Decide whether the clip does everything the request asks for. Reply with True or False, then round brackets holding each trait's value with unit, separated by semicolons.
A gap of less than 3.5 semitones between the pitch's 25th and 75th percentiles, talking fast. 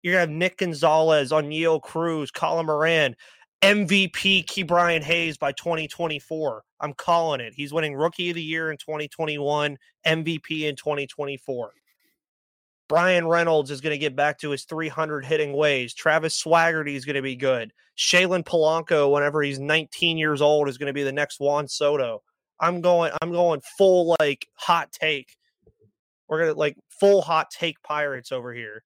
False (2.6 semitones; 160 wpm)